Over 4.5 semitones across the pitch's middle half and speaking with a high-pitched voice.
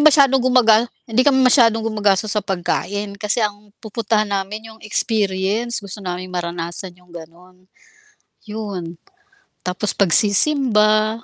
No: average, 3.2 semitones; high, 210 Hz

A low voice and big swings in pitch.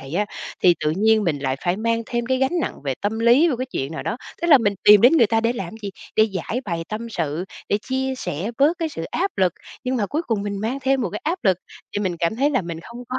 No: high, 220 Hz; wide, 5.9 semitones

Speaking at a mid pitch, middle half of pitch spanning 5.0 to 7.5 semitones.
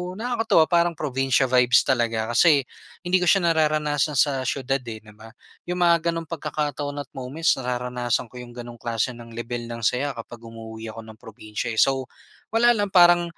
No: low, 130 Hz; average, 5.3 semitones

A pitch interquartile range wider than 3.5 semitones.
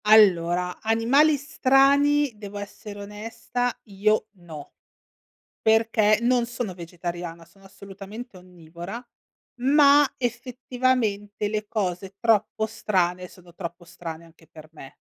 Yes: average, 5.2 semitones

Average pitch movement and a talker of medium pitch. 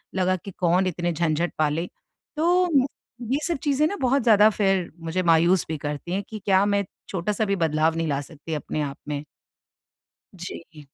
Yes: average, 4.0 semitones; medium, 175 Hz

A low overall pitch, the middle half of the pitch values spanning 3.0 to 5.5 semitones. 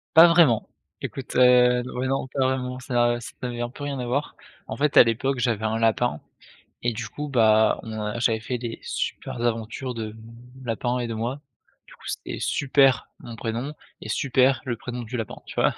No: low, 120 Hz; narrow, 2.4 semitones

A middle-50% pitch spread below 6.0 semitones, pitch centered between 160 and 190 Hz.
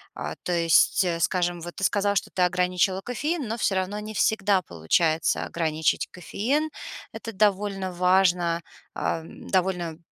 Yes: average, 2.8 semitones; medium, 185 Hz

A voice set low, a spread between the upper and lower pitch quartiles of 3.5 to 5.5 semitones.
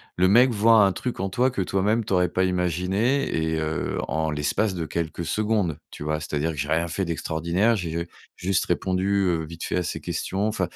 Yes: very low, 90 Hz; average, 3.9 semitones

